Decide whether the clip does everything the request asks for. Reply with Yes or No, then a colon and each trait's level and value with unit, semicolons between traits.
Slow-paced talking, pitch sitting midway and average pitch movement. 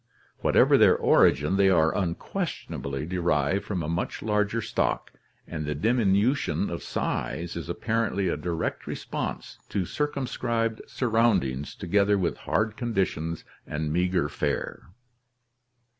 No: slow, 120 wpm; very low, 95 Hz; average, 4.8 semitones